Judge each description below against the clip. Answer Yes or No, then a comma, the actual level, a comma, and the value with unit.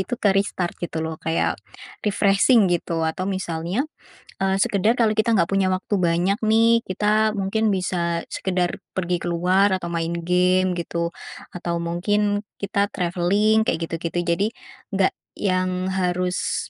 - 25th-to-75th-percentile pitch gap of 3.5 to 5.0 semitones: No, average, 2.8 semitones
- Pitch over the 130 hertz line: Yes, medium, 185 Hz